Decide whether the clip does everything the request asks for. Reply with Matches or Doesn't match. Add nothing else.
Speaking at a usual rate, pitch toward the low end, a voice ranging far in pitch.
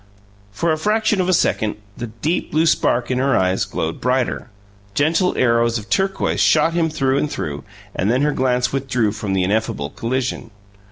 Matches